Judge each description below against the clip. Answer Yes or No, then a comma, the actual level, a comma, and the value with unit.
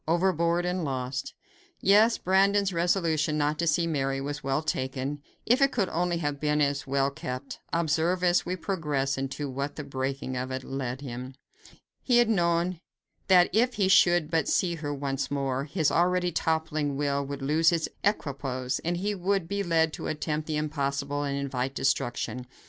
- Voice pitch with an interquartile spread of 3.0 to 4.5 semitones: Yes, average, 4.1 semitones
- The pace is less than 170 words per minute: No, average, 175 wpm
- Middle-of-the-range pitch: Yes, medium, 150 Hz